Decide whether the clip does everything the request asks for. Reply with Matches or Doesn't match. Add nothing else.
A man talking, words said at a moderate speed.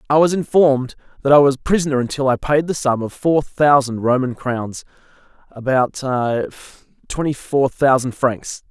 Matches